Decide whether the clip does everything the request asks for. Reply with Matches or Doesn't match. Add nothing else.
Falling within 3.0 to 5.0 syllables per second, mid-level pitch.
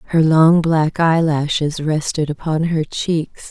Matches